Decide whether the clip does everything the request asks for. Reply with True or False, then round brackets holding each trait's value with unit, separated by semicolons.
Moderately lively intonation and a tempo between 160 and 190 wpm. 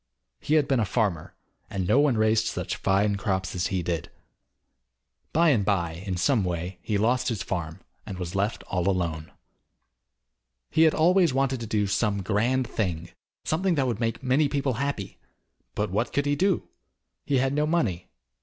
False (6.4 semitones; 180 wpm)